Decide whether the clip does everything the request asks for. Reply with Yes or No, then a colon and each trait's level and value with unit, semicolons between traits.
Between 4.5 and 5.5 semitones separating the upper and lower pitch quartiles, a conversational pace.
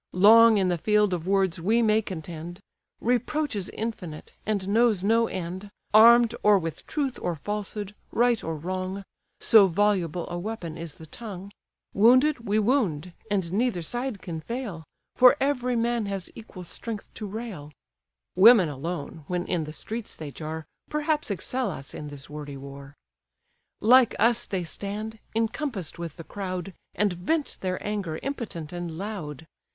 Yes: average, 5.1 semitones; average, 155 wpm